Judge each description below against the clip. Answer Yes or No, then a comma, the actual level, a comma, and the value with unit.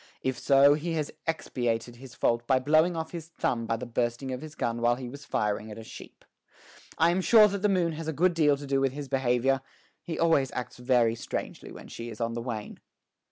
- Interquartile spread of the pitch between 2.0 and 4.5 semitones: No, average, 5.1 semitones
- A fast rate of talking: Yes, fast, 230 wpm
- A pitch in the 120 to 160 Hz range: Yes, low, 135 Hz